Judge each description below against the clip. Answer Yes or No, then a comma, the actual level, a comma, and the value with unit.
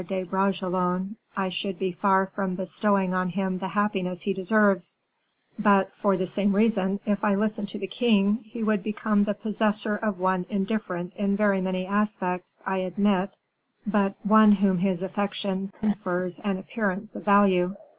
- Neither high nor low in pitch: No, high, 195 Hz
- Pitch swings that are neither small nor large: No, narrow, 1.9 semitones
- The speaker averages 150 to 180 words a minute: Yes, average, 165 wpm